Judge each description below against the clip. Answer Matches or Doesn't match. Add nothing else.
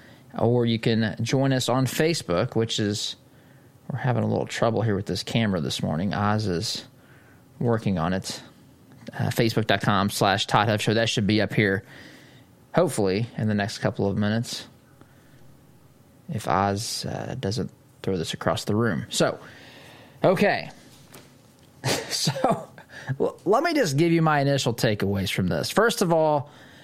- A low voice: Matches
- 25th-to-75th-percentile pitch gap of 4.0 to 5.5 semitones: Matches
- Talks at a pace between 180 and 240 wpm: Doesn't match